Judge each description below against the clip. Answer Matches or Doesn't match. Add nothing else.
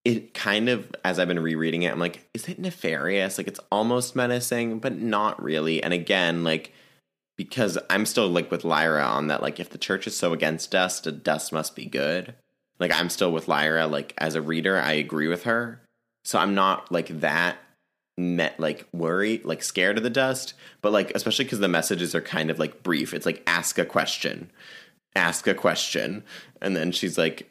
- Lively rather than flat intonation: Matches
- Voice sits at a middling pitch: Doesn't match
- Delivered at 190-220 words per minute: Matches